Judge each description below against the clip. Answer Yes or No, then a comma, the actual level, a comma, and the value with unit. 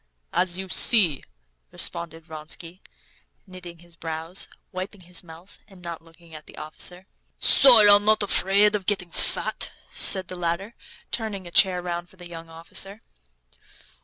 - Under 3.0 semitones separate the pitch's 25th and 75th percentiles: Yes, narrow, 2.6 semitones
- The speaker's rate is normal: Yes, average, 150 wpm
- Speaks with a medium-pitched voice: Yes, medium, 180 Hz